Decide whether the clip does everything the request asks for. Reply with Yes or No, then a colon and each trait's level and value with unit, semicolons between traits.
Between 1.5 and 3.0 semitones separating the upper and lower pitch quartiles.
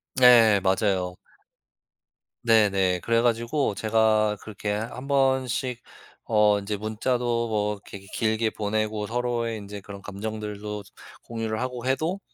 Yes: narrow, 2.4 semitones